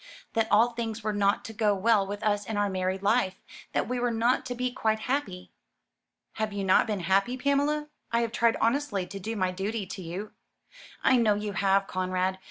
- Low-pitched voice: No, high, 210 Hz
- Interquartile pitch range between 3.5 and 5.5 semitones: No, average, 3.1 semitones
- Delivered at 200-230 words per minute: Yes, fast, 205 wpm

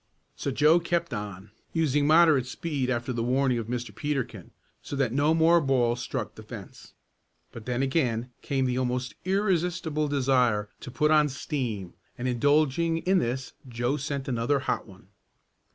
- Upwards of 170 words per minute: No, average, 165 wpm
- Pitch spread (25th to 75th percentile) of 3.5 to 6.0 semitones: Yes, average, 3.9 semitones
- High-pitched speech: No, low, 135 Hz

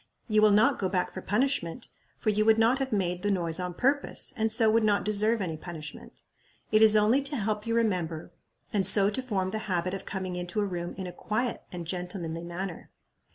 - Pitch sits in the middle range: No, high, 200 Hz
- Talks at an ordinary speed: No, fast, 215 wpm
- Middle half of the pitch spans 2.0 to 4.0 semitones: Yes, average, 3.6 semitones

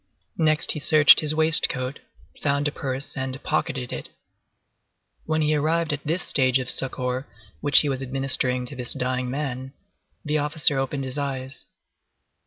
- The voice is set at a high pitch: No, low, 135 Hz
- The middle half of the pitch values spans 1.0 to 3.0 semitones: Yes, narrow, 2.6 semitones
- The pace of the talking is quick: No, average, 160 wpm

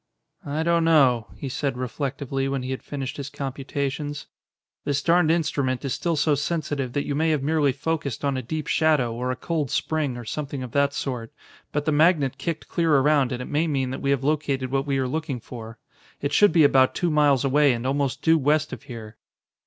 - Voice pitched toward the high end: No, medium, 140 Hz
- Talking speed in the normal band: No, fast, 215 wpm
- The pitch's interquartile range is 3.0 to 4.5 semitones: No, narrow, 2.6 semitones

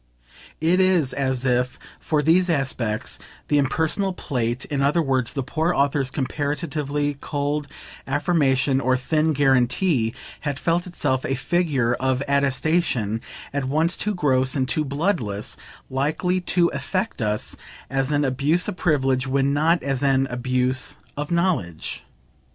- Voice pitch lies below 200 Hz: Yes, medium, 140 Hz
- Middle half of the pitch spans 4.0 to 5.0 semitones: No, average, 3.5 semitones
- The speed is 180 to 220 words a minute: No, average, 140 wpm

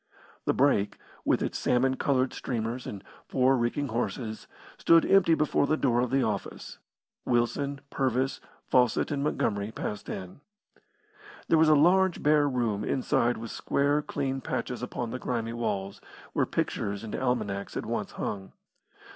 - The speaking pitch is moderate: No, low, 125 Hz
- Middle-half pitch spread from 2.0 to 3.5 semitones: No, average, 4.0 semitones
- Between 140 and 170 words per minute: Yes, average, 150 wpm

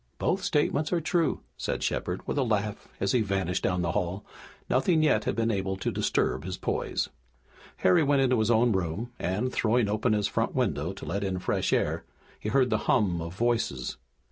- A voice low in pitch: Yes, low, 105 Hz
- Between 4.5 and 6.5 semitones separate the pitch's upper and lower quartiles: Yes, average, 5.2 semitones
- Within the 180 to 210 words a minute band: Yes, average, 195 wpm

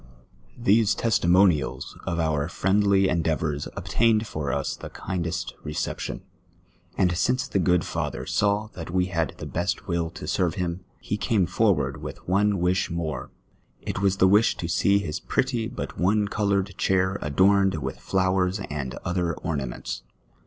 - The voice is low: Yes, very low, 95 Hz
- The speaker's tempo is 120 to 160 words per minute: Yes, average, 150 wpm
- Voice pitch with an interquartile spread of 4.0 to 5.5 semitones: No, average, 3.2 semitones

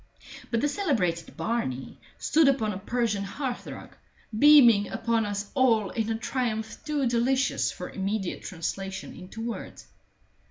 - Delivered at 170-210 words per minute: No, slow, 135 wpm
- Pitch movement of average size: Yes, average, 4.4 semitones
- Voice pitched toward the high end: Yes, high, 225 Hz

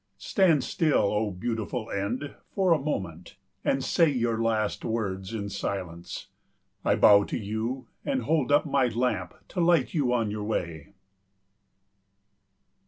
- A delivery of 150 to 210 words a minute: No, average, 140 wpm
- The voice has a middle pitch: No, low, 115 Hz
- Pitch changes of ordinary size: No, wide, 5.8 semitones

